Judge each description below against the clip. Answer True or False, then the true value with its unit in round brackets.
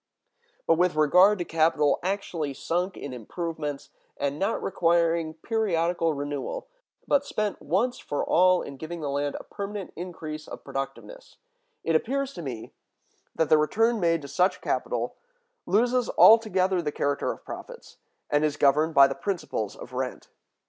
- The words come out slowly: False (155 wpm)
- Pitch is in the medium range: True (165 Hz)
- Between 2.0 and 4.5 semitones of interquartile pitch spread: False (4.9 semitones)